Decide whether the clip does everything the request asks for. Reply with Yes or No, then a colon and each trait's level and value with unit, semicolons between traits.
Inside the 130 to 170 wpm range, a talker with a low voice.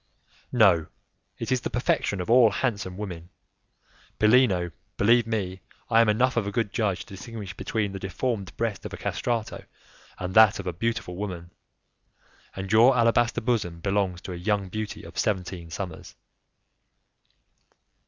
Yes: average, 155 wpm; low, 100 Hz